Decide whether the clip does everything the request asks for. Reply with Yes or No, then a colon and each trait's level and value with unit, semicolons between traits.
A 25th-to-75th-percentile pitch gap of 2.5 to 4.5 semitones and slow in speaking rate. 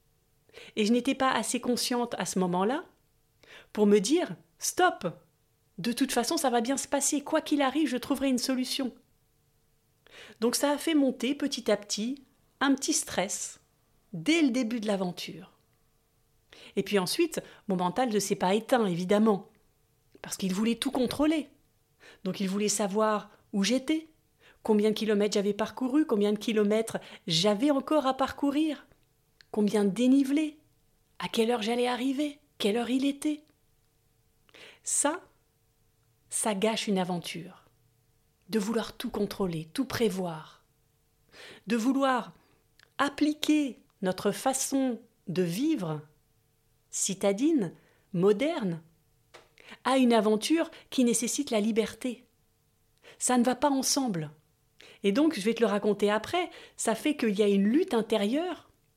No: wide, 5.4 semitones; slow, 140 wpm